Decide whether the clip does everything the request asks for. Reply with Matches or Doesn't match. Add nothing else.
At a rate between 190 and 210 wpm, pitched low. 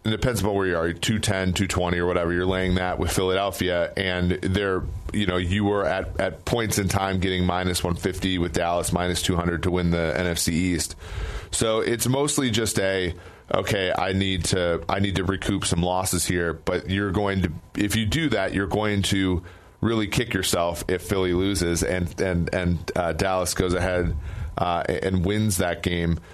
Matches